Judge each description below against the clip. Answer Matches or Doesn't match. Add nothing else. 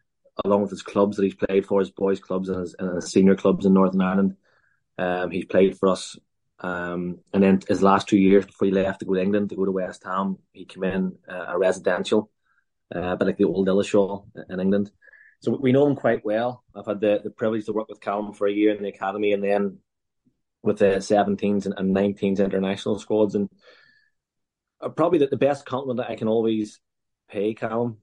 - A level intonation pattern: Matches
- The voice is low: Matches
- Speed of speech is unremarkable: Doesn't match